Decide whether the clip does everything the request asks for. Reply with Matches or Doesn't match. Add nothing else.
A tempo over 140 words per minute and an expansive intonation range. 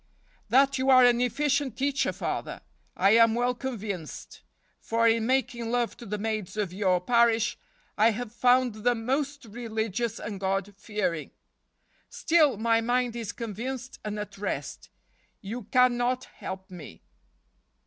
Doesn't match